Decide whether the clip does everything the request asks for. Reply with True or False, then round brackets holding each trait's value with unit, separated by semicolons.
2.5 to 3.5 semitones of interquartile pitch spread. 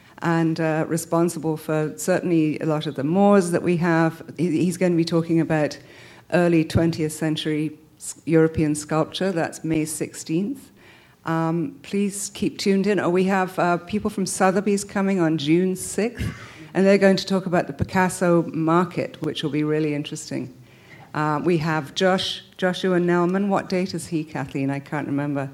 True (3.0 semitones)